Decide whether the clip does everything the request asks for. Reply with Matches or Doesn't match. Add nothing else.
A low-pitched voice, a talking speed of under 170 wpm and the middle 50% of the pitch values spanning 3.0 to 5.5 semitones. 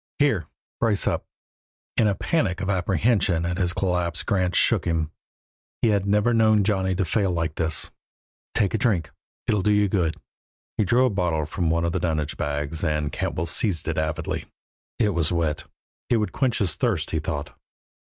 Doesn't match